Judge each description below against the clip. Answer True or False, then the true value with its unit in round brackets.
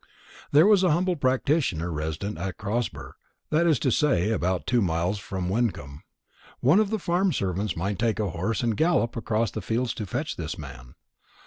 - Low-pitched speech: True (110 Hz)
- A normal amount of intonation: False (8.4 semitones)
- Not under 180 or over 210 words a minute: True (185 wpm)